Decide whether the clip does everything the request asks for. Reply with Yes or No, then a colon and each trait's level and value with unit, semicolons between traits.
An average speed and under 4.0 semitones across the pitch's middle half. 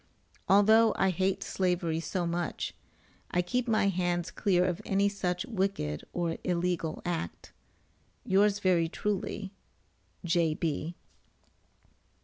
No: slow, 110 wpm; narrow, 2.5 semitones